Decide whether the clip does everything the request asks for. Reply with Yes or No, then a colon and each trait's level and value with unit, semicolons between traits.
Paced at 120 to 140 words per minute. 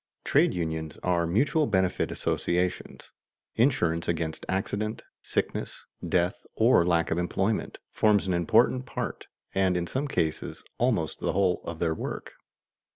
Yes: slow, 135 wpm